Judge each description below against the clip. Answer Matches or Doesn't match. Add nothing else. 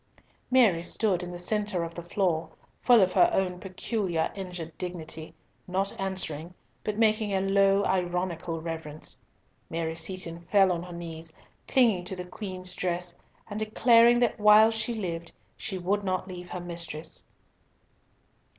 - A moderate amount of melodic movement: Matches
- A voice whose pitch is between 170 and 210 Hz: Matches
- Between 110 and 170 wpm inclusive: Matches